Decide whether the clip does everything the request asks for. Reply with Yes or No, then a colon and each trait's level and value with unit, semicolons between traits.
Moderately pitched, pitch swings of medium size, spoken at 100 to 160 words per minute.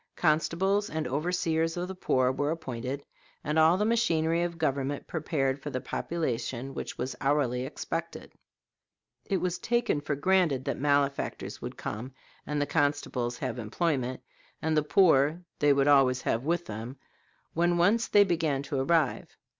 Yes: medium, 150 Hz; average, 4.3 semitones; average, 155 wpm